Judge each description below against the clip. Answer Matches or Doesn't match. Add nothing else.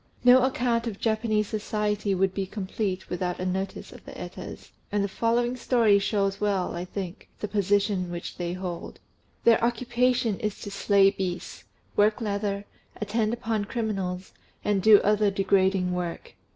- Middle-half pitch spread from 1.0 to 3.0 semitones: Matches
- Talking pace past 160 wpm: Doesn't match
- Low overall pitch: Doesn't match